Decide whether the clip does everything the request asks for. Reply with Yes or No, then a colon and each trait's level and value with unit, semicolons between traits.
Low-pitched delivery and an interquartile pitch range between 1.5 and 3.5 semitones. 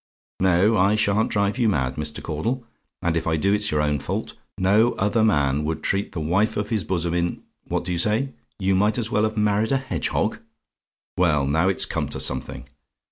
No: very low, 95 Hz; average, 4.8 semitones